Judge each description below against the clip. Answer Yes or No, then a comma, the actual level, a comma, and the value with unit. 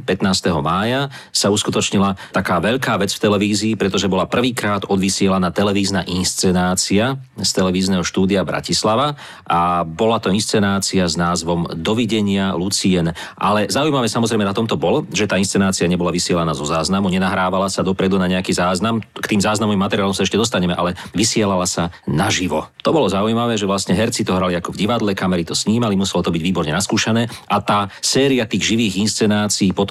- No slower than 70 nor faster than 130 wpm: No, fast, 165 wpm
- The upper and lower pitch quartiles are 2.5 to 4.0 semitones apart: Yes, average, 2.8 semitones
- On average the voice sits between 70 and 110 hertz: Yes, low, 100 Hz